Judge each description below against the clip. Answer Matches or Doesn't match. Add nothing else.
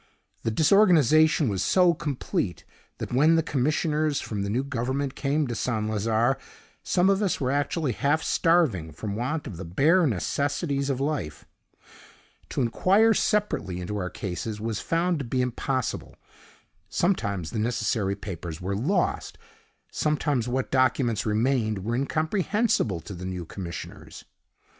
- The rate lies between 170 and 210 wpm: Doesn't match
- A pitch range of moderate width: Doesn't match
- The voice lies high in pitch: Doesn't match